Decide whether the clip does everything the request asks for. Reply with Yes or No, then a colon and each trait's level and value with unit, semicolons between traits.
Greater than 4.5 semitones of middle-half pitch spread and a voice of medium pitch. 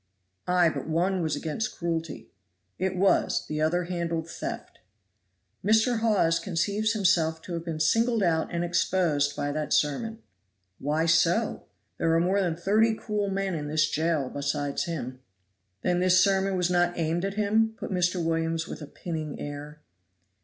No: average, 3.5 semitones; medium, 170 Hz